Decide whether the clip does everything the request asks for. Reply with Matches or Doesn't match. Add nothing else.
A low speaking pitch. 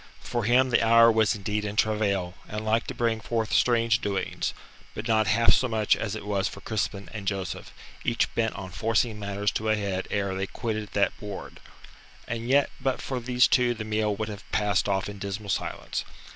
Matches